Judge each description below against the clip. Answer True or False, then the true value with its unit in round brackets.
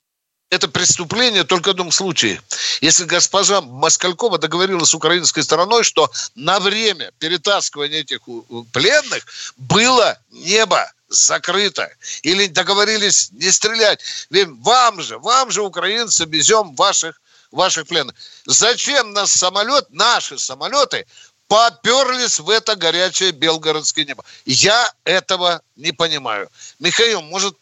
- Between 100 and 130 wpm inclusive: True (120 wpm)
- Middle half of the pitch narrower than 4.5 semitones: False (4.8 semitones)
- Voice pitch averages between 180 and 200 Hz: True (185 Hz)